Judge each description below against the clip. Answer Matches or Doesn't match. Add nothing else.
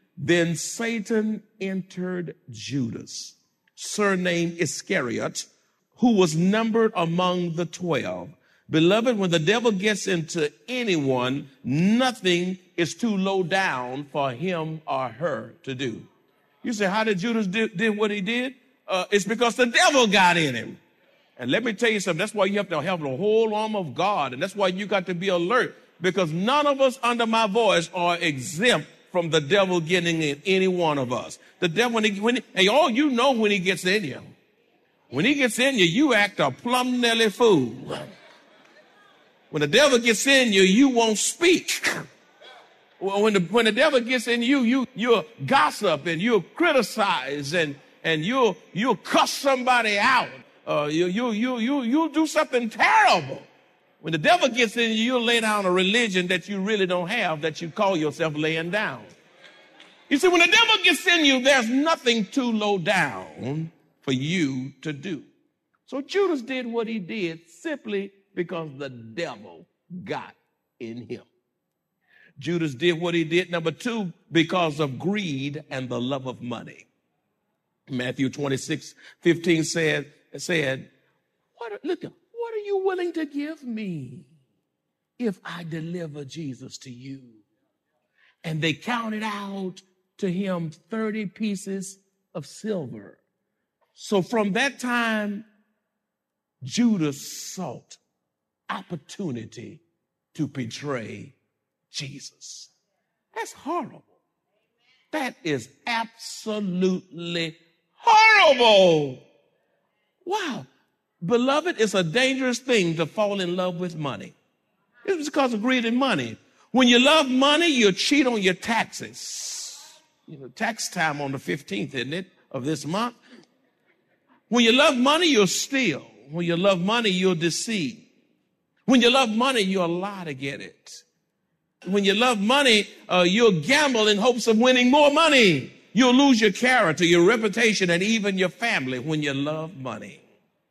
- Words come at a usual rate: Matches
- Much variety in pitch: Matches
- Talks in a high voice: Matches